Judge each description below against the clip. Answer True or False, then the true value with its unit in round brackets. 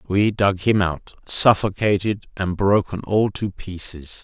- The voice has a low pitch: True (100 Hz)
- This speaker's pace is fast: False (140 wpm)